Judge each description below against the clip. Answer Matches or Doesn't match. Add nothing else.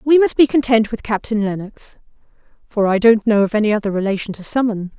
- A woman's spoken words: Matches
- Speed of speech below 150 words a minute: Doesn't match